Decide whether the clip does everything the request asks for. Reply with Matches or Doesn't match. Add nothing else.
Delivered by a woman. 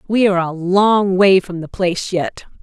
Matches